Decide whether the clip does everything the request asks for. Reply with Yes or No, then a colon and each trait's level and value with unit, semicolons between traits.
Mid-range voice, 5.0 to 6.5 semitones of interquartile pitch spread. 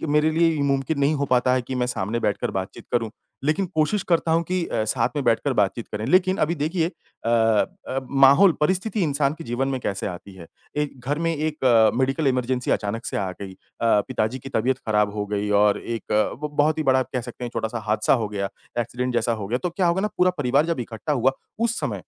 No: low, 130 Hz; wide, 5.6 semitones